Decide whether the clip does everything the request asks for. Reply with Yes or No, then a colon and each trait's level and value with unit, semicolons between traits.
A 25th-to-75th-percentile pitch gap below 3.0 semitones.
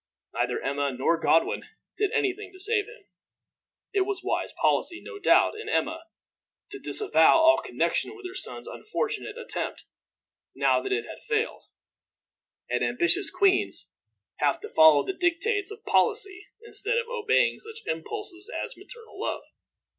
No: average, 3.6 semitones